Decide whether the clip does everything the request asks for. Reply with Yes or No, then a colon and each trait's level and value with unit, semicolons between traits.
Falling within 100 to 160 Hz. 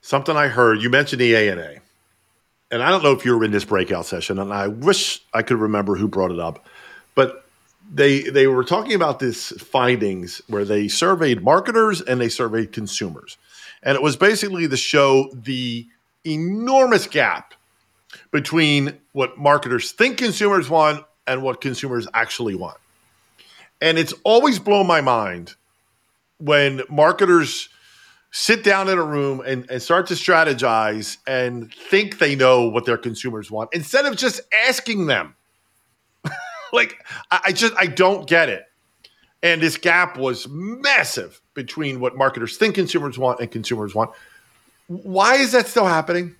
Yes: medium, 140 Hz